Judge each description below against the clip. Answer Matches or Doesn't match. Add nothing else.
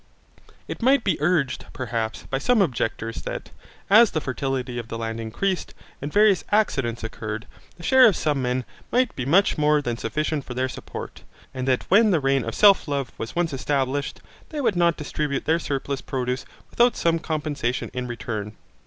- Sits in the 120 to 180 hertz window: Matches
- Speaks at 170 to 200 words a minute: Matches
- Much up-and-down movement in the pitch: Matches